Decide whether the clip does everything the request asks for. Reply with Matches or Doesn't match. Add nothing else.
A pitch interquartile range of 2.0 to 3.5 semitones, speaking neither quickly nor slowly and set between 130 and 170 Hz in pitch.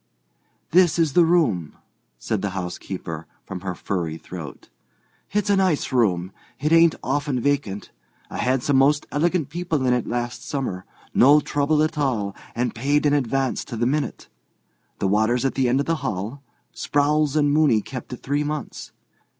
Doesn't match